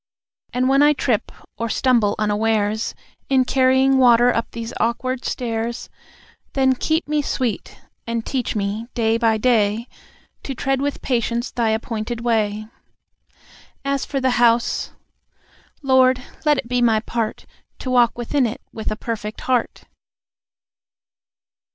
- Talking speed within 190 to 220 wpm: No, slow, 135 wpm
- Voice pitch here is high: Yes, high, 240 Hz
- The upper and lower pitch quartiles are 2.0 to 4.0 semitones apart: Yes, narrow, 2.6 semitones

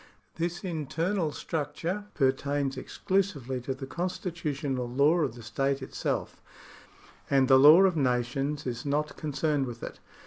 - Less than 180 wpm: Yes, average, 140 wpm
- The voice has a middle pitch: Yes, medium, 145 Hz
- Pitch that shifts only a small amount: No, average, 3.8 semitones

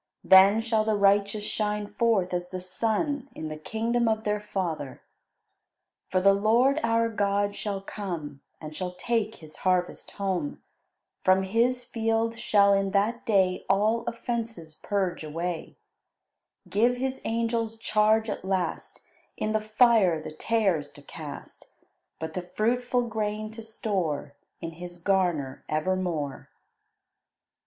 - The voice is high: Yes, high, 205 Hz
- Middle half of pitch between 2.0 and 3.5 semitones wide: No, average, 3.9 semitones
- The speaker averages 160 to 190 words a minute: No, slow, 135 wpm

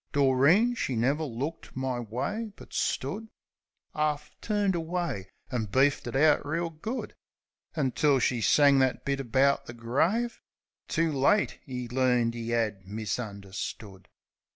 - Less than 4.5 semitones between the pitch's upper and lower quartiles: No, average, 5.2 semitones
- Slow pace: Yes, slow, 130 wpm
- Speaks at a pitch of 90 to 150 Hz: Yes, low, 135 Hz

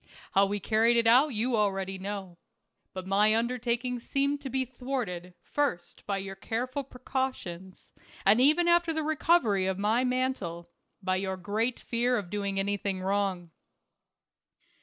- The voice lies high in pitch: Yes, high, 215 Hz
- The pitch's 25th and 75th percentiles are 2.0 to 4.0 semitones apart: No, average, 4.8 semitones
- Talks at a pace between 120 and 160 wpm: Yes, average, 150 wpm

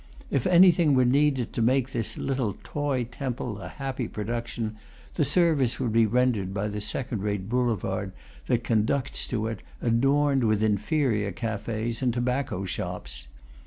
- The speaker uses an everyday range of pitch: Yes, average, 4.0 semitones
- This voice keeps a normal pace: Yes, average, 150 wpm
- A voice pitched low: Yes, low, 120 Hz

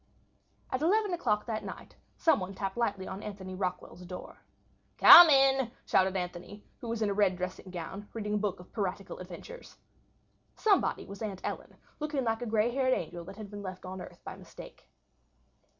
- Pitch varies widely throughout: No, average, 4.3 semitones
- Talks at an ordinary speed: Yes, average, 180 wpm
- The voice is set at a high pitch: Yes, high, 205 Hz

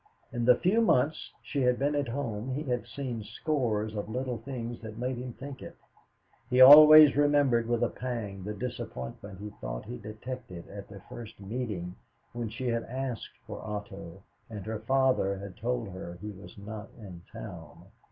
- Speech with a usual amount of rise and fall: Yes, average, 3.9 semitones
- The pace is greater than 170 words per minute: Yes, average, 180 wpm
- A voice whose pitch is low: Yes, low, 115 Hz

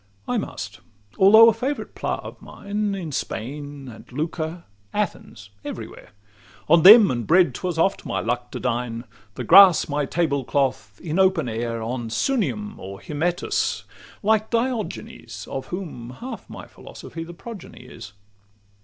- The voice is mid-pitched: Yes, medium, 160 Hz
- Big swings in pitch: Yes, wide, 8.2 semitones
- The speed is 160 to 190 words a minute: No, average, 150 wpm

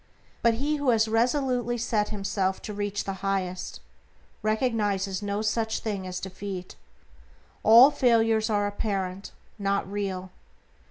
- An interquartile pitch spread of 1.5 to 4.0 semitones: Yes, narrow, 2.6 semitones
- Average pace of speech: No, slow, 125 wpm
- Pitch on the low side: No, high, 205 Hz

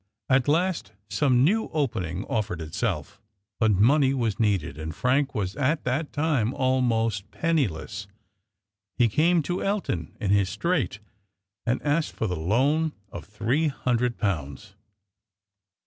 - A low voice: Yes, low, 120 Hz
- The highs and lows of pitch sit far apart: Yes, wide, 6.6 semitones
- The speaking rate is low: Yes, slow, 130 wpm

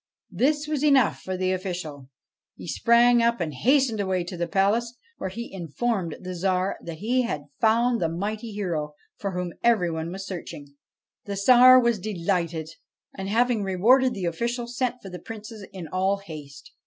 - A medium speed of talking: Yes, average, 175 wpm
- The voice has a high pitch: Yes, high, 195 Hz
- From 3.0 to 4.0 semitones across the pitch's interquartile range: No, average, 5.2 semitones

